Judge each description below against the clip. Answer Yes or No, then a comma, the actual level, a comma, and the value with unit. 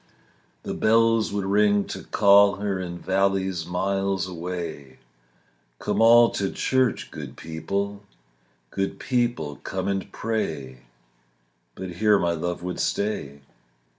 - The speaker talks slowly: Yes, slow, 120 wpm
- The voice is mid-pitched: No, very low, 95 Hz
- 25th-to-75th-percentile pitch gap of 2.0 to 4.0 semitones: Yes, average, 2.9 semitones